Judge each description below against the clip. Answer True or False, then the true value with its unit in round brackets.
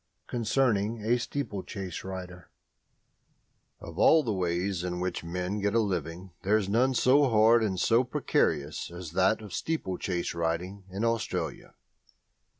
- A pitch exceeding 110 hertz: False (100 Hz)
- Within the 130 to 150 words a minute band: True (140 wpm)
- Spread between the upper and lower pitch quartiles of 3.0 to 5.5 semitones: True (4.1 semitones)